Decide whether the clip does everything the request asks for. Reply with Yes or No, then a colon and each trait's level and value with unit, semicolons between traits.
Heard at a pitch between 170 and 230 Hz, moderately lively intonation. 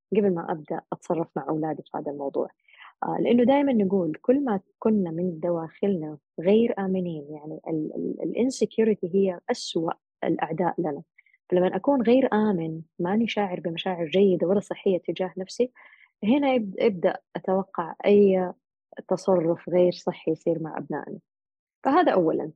Yes: high, 190 Hz; average, 4.0 semitones